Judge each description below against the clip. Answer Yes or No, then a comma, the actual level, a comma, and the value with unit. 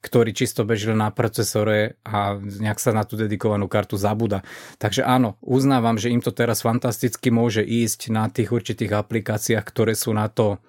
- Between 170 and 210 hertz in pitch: No, low, 115 Hz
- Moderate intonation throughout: No, narrow, 2.1 semitones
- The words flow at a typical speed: No, fast, 175 wpm